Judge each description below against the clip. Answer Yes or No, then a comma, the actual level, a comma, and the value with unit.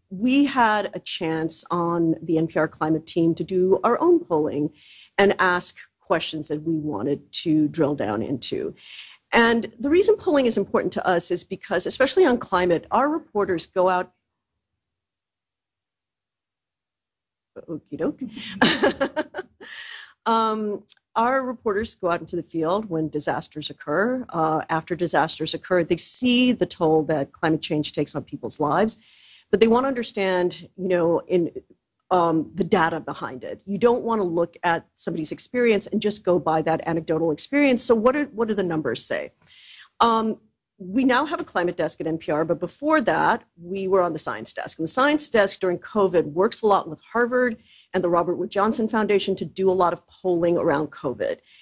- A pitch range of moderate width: No, wide, 5.7 semitones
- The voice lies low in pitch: No, medium, 185 Hz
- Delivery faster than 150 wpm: Yes, average, 170 wpm